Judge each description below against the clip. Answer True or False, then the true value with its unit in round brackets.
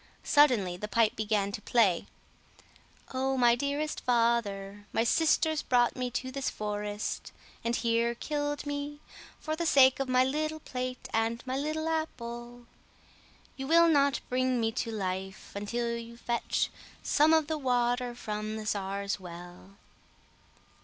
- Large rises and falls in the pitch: False (4.8 semitones)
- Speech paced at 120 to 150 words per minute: True (145 wpm)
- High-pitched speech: True (240 Hz)